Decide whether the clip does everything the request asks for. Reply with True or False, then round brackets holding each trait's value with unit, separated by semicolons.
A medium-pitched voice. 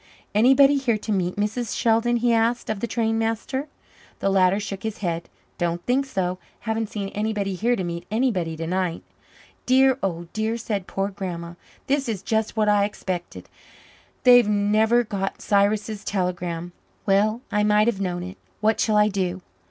False (210 Hz)